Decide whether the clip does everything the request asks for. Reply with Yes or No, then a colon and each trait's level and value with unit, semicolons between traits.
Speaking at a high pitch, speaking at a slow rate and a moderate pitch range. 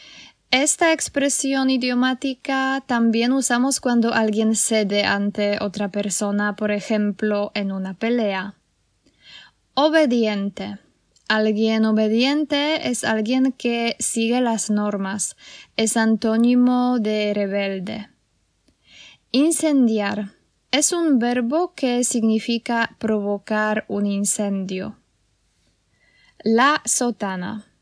Yes: high, 225 Hz; slow, 85 wpm; average, 3.5 semitones